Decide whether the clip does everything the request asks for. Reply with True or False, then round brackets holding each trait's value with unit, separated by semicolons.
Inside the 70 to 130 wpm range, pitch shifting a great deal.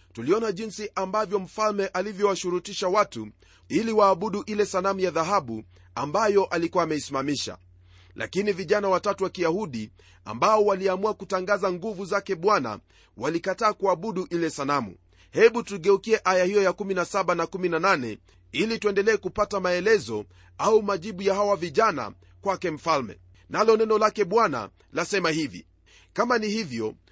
True (125 wpm; 6.9 semitones)